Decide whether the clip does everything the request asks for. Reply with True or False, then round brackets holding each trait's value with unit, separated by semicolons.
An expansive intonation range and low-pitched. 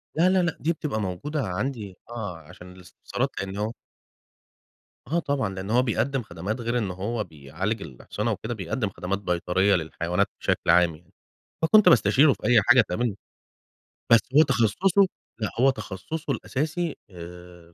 True (6.5 semitones; 105 Hz)